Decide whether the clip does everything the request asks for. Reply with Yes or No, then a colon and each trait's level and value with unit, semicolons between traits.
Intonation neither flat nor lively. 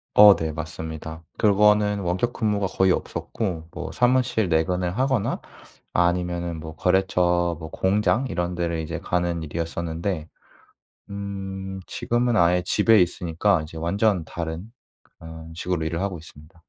Yes: average, 3.5 semitones